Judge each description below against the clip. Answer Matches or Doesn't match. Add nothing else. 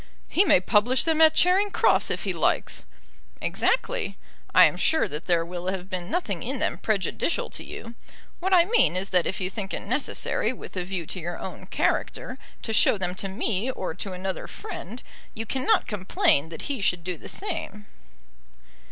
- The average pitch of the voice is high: Matches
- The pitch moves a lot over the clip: Matches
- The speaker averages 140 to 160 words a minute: Doesn't match